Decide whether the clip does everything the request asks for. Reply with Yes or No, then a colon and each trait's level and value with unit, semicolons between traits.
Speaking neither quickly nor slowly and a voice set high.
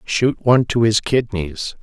No: average, 165 wpm; low, 110 Hz